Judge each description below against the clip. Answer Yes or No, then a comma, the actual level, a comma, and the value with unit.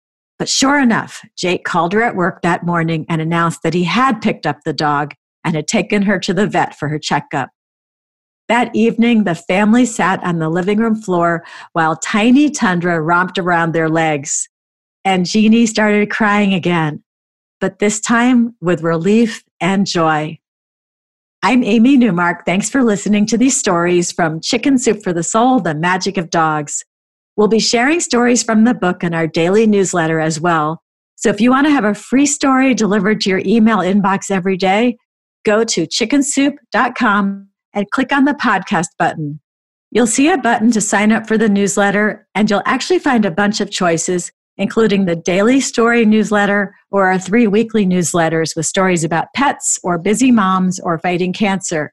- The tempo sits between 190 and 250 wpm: No, average, 175 wpm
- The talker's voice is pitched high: Yes, high, 200 Hz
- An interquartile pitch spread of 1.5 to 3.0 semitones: No, average, 4.7 semitones